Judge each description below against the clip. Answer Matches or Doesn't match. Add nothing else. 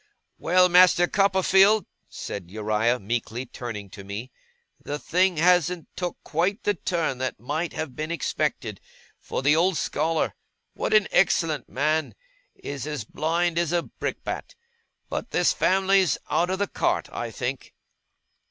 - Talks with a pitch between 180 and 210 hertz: Doesn't match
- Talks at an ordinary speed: Matches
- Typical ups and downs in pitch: Doesn't match